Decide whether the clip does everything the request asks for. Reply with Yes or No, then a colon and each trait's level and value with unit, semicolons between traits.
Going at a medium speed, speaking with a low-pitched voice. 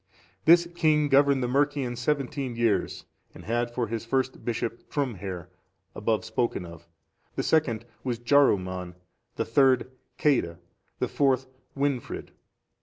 No: slow, 125 wpm; low, 125 Hz